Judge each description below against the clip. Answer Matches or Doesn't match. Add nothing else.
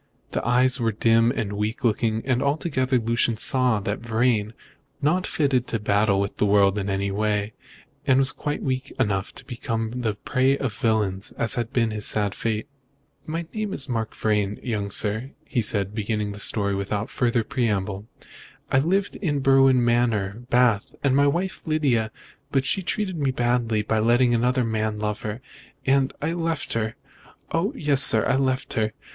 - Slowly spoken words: Doesn't match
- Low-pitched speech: Matches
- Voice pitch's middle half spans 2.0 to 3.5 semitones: Doesn't match